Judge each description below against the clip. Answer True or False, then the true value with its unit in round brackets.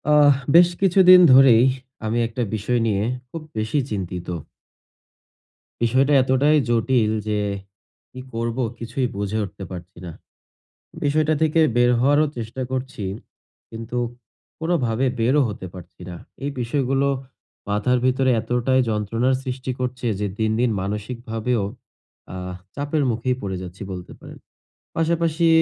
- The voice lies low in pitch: True (125 Hz)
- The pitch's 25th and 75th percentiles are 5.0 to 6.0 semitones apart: False (4.1 semitones)